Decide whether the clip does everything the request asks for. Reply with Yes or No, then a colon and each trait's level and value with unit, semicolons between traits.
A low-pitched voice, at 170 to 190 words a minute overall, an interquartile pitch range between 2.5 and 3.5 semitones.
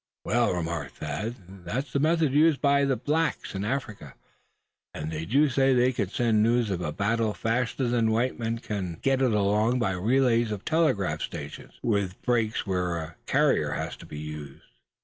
No: low, 115 Hz; average, 175 wpm; wide, 5.5 semitones